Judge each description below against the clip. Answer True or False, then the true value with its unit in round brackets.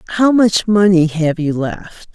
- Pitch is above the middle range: False (180 Hz)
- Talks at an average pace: True (170 wpm)